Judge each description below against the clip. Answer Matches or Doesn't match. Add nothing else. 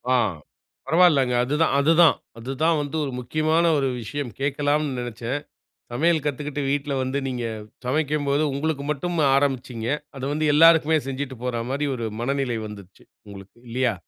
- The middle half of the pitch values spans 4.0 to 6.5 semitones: Doesn't match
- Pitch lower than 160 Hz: Matches